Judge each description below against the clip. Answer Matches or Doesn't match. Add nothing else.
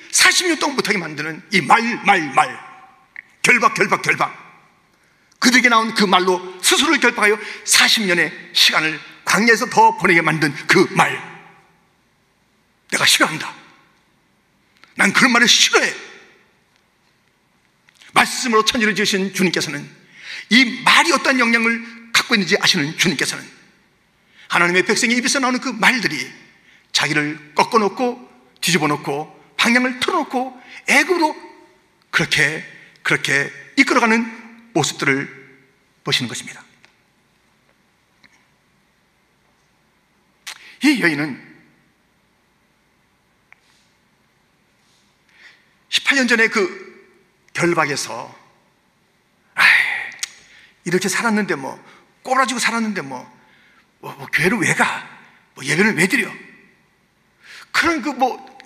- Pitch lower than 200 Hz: Doesn't match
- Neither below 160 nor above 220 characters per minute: Matches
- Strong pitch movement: Matches